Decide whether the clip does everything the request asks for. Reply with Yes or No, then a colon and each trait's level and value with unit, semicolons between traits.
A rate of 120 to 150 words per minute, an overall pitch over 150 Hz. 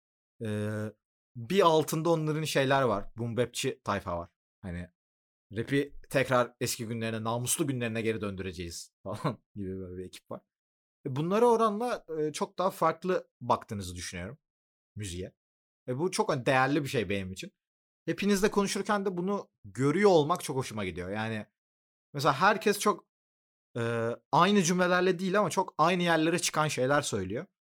No: average, 135 wpm; low, 125 Hz